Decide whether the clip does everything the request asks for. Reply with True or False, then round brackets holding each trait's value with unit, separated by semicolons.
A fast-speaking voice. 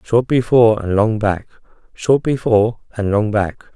False (160 wpm)